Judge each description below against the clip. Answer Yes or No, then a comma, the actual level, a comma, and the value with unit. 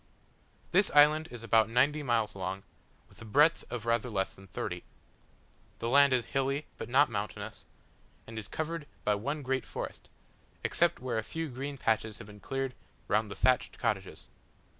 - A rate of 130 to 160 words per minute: No, average, 170 wpm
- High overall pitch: No, low, 120 Hz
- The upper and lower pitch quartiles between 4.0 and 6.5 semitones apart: Yes, average, 4.6 semitones